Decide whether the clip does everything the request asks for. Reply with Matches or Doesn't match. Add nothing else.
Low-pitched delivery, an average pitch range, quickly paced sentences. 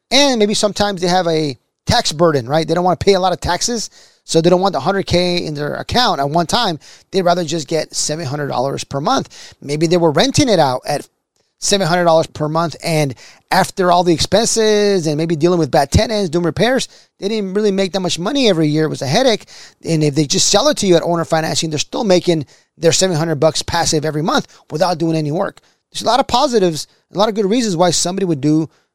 Doesn't match